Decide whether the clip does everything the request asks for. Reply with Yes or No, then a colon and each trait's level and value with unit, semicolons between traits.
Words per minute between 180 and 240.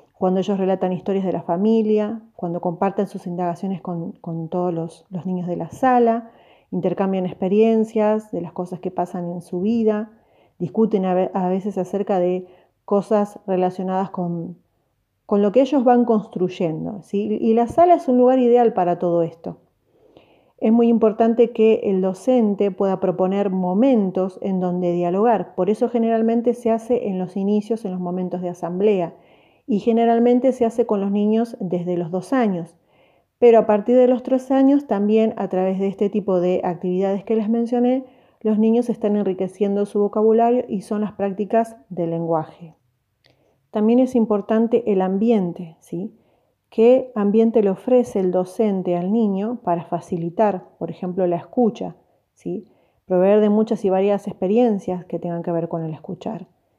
No: average, 165 wpm